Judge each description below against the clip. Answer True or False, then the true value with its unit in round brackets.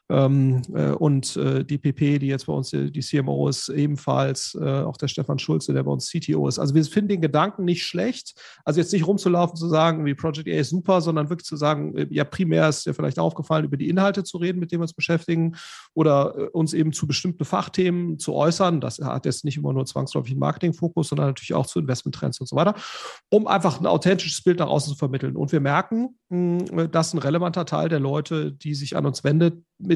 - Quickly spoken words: True (215 wpm)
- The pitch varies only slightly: False (3.6 semitones)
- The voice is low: False (155 Hz)